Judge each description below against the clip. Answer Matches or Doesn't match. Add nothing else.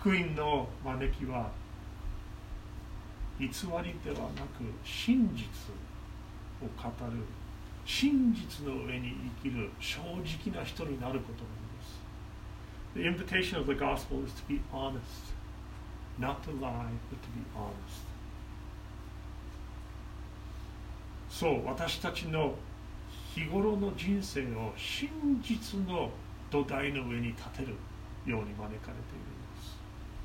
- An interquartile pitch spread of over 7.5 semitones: Doesn't match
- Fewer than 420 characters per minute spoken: Matches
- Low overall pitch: Matches